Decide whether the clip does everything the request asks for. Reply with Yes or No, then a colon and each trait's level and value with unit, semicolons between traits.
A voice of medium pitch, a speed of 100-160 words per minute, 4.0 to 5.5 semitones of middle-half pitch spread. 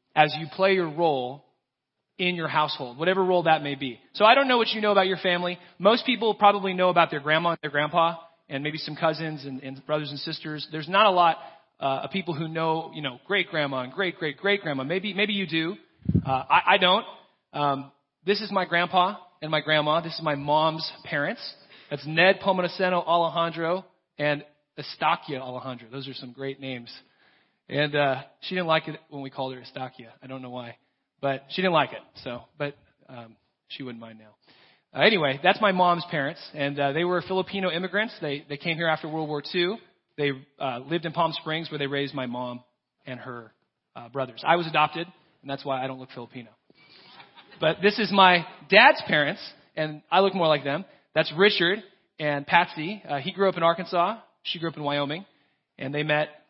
No: medium, 155 Hz; fast, 205 wpm; average, 4.3 semitones